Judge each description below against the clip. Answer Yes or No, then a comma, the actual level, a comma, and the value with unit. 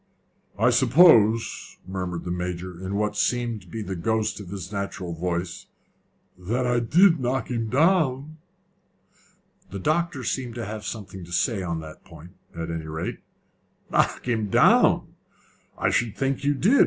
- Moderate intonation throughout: No, wide, 5.7 semitones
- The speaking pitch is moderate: No, low, 110 Hz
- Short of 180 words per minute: Yes, average, 155 wpm